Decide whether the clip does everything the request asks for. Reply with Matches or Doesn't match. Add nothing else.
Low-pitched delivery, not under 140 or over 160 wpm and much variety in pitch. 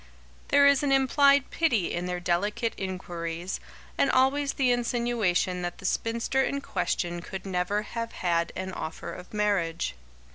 Doesn't match